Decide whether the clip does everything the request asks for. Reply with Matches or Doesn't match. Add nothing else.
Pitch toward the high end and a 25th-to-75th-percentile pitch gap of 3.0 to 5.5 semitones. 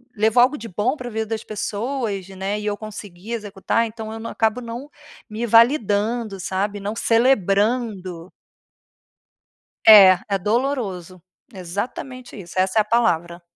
Matches